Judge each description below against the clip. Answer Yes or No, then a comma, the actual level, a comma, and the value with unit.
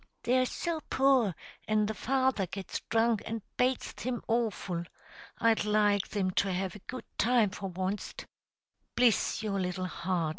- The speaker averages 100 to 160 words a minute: Yes, average, 150 wpm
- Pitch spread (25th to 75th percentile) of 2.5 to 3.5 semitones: No, average, 4.2 semitones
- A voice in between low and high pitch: No, high, 215 Hz